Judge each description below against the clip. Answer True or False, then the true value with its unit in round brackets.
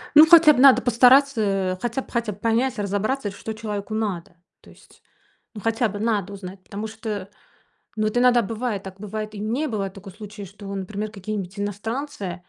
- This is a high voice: True (215 Hz)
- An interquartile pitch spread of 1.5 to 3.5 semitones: True (2.9 semitones)